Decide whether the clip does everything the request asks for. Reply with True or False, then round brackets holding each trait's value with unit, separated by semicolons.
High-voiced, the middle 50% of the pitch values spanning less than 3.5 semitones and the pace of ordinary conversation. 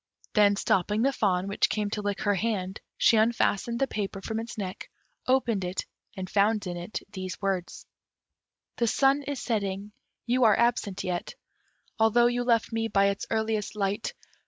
True (210 Hz; 3.0 semitones; 170 wpm)